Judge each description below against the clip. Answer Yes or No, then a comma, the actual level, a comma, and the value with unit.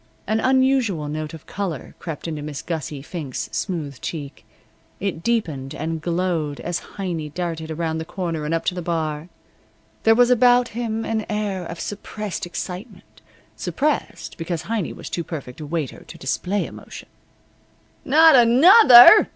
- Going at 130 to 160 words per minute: Yes, average, 150 wpm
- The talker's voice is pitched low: No, medium, 175 Hz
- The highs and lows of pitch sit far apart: Yes, wide, 6.0 semitones